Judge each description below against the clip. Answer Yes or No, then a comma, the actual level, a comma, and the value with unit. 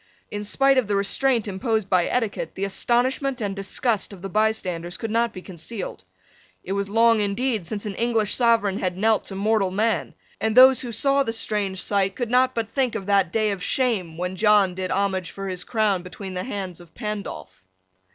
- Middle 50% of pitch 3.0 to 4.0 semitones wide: Yes, average, 3.3 semitones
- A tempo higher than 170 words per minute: Yes, average, 200 wpm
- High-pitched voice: Yes, high, 205 Hz